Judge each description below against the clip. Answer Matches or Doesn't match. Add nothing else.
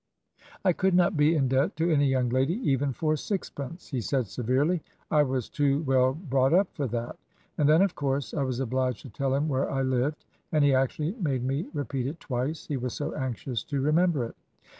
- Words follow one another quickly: Matches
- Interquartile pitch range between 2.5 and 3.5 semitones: Matches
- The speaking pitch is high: Doesn't match